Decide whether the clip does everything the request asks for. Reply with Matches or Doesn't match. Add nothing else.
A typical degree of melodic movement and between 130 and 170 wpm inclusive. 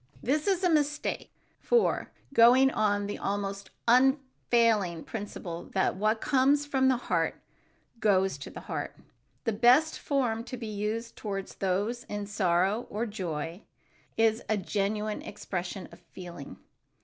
Matches